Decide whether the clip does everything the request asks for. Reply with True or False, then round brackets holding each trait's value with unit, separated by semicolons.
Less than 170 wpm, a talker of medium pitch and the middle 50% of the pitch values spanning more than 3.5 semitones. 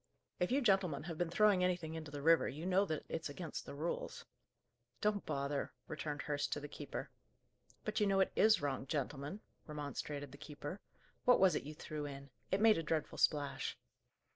False (190 wpm; 155 Hz; 4.7 semitones)